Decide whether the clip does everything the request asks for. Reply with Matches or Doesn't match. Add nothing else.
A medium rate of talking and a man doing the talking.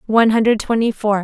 Doesn't match